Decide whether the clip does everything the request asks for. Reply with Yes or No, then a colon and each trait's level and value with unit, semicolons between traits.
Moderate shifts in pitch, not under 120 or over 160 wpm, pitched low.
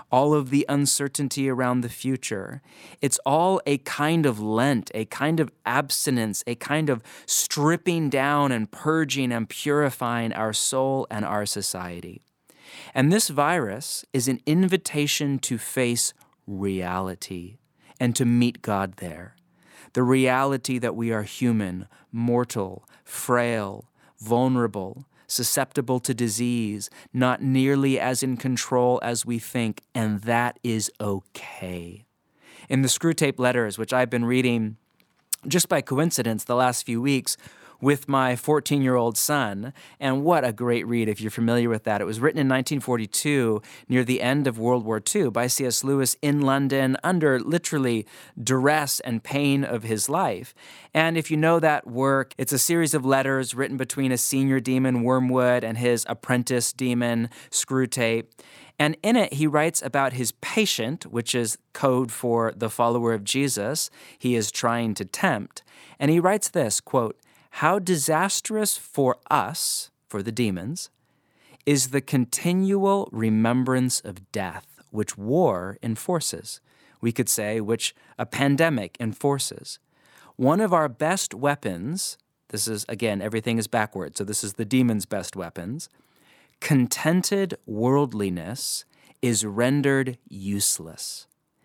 Yes: average, 3.6 semitones; average, 145 wpm; low, 125 Hz